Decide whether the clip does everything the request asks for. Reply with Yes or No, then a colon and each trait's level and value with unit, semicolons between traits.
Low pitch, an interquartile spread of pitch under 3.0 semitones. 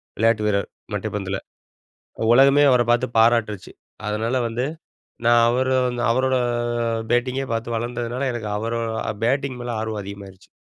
Yes: low, 120 Hz; narrow, 2.5 semitones